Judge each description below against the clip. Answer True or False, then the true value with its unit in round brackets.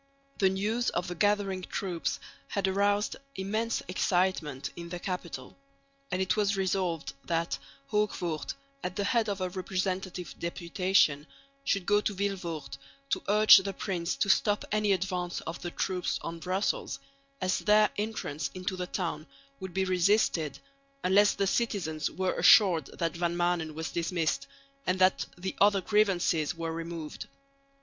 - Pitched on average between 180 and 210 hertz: True (185 Hz)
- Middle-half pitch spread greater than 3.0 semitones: False (2.7 semitones)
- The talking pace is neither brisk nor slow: True (150 wpm)